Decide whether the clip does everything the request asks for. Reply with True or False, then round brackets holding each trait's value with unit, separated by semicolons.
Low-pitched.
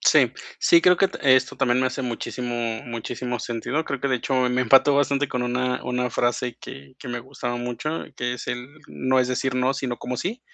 True (125 Hz)